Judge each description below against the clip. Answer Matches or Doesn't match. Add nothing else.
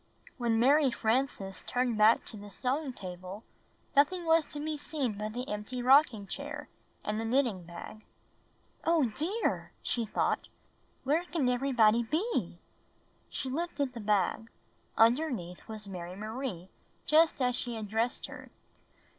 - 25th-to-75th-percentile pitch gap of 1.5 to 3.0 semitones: Doesn't match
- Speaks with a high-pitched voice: Matches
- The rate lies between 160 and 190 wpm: Doesn't match